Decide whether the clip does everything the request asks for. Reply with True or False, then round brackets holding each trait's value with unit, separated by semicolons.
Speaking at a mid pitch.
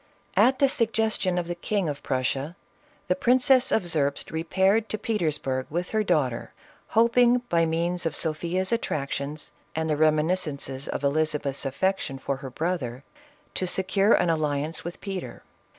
True (170 Hz)